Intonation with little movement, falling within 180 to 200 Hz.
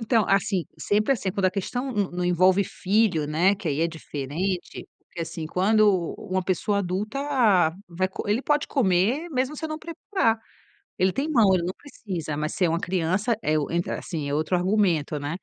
No: average, 4.1 semitones; high, 190 Hz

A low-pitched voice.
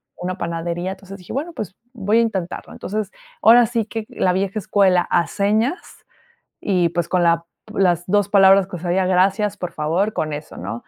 No: high, 190 Hz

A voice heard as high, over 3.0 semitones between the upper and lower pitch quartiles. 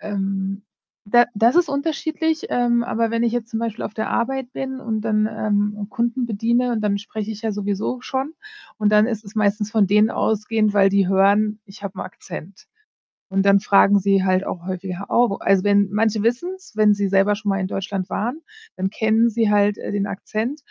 No: high, 210 Hz; average, 2.7 semitones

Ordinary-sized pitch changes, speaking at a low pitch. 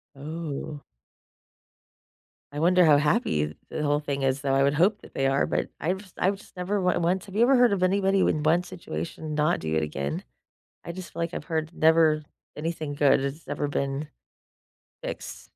No: average, 4.3 semitones; medium, 155 Hz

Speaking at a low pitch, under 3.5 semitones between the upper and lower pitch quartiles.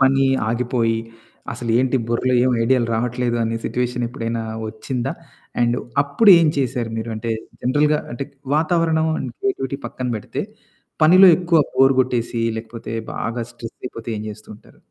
Yes: low, 125 Hz; average, 3.0 semitones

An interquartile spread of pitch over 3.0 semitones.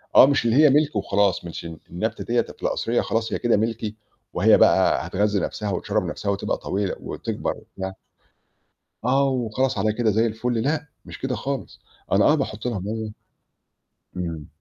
Yes: average, 3.6 semitones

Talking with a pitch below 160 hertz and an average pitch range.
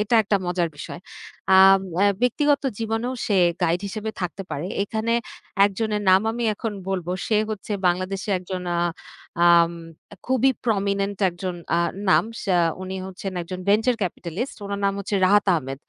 No: high, 195 Hz; average, 3.0 semitones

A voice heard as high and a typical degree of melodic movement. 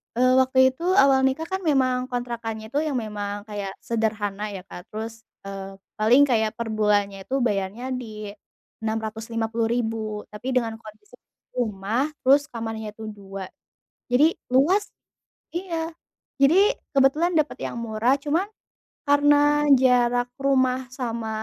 Yes: high, 235 Hz; average, 3.4 semitones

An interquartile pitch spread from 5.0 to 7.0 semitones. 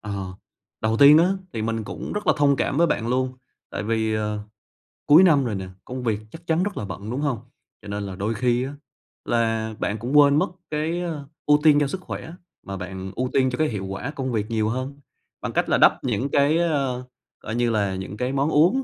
Yes: average, 5.3 semitones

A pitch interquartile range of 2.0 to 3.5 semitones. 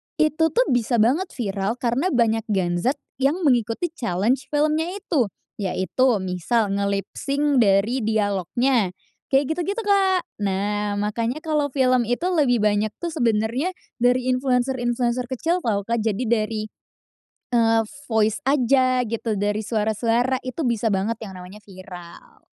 No: average, 4.3 semitones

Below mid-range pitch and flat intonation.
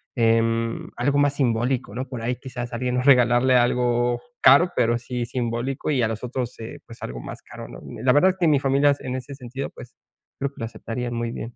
Yes: low, 125 Hz; narrow, 2.2 semitones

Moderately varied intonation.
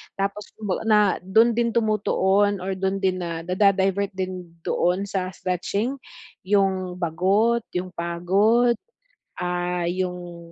No: narrow, 2.3 semitones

